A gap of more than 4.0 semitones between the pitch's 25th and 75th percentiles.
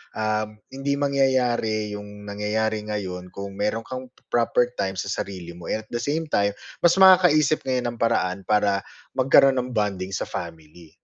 Yes: average, 4.5 semitones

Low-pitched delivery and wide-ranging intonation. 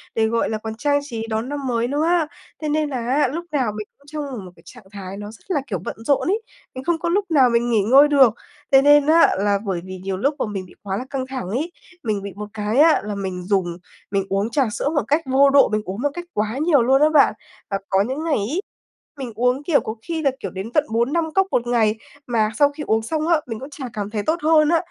No: very high, 250 Hz; wide, 5.8 semitones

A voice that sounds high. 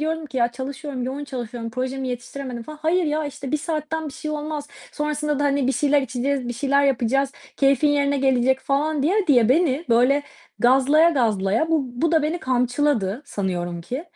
Yes: very high, 275 Hz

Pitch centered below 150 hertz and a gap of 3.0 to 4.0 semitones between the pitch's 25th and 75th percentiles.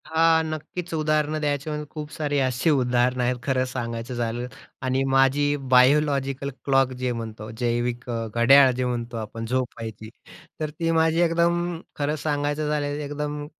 Yes: medium, 140 Hz; average, 3.5 semitones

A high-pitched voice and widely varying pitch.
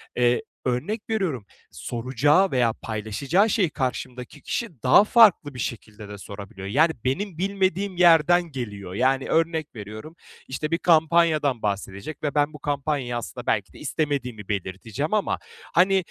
No: medium, 140 Hz; wide, 6.4 semitones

